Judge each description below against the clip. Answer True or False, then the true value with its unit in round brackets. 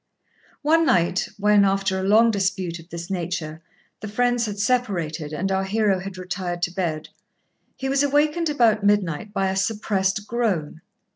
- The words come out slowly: False (160 wpm)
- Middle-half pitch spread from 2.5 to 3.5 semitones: False (3.9 semitones)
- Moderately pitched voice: False (195 Hz)